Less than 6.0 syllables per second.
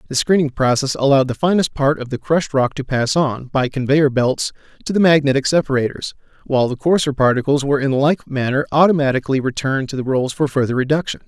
No: 6.3 syllables/s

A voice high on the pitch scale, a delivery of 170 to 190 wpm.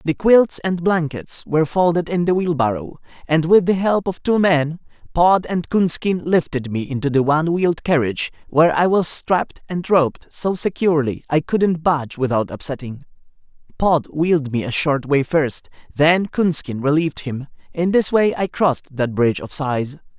No: medium, 160 Hz; average, 175 wpm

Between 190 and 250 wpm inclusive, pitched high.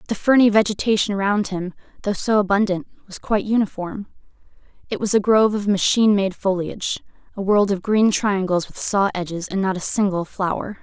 No: average, 170 wpm; high, 200 Hz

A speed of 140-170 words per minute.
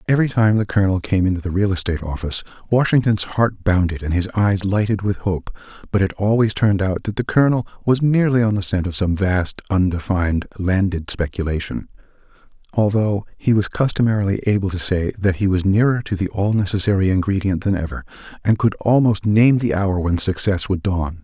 No: average, 185 wpm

